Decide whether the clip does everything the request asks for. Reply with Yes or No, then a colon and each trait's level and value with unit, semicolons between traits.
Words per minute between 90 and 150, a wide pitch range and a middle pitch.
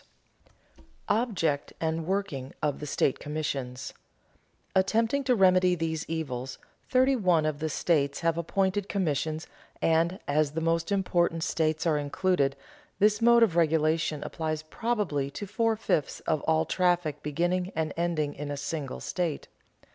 No: average, 145 wpm; average, 3.8 semitones; medium, 165 Hz